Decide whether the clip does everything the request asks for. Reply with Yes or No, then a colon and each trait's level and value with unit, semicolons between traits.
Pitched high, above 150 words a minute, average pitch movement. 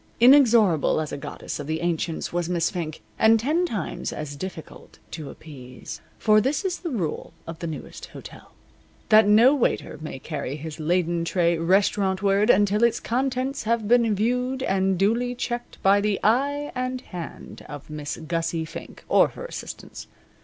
No: high, 195 Hz; average, 165 wpm; wide, 6.6 semitones